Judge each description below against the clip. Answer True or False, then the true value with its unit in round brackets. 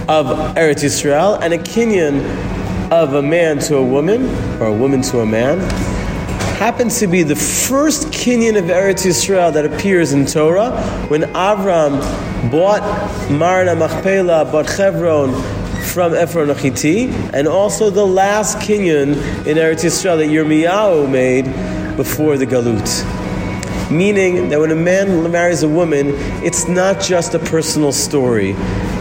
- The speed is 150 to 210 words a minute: False (140 wpm)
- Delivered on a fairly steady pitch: False (5.0 semitones)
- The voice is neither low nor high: True (160 Hz)